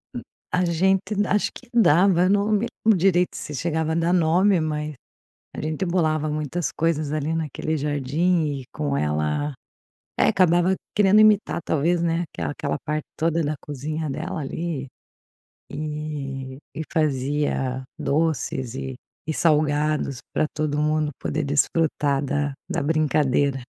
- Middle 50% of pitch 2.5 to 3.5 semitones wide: Yes, average, 3.0 semitones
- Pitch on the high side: No, medium, 155 Hz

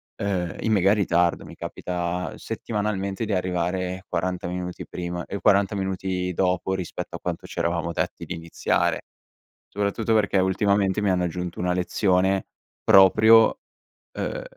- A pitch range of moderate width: No, narrow, 2.0 semitones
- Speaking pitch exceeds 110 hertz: No, very low, 95 Hz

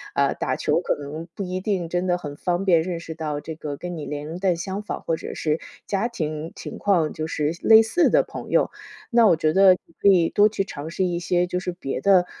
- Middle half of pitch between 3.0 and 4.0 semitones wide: Yes, average, 3.5 semitones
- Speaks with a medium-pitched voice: Yes, medium, 175 Hz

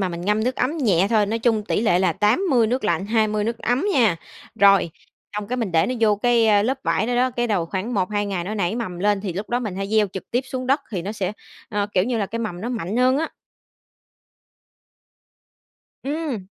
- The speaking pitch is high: Yes, high, 215 Hz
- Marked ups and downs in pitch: No, average, 3.6 semitones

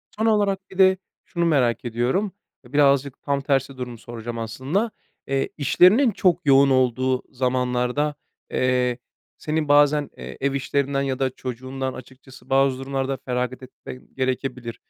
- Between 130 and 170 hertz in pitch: Yes, low, 135 Hz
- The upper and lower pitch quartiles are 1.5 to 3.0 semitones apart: Yes, narrow, 2.4 semitones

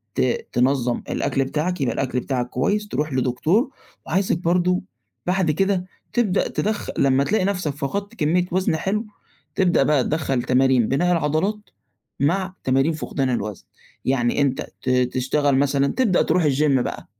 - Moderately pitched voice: Yes, medium, 150 Hz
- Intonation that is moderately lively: No, wide, 5.7 semitones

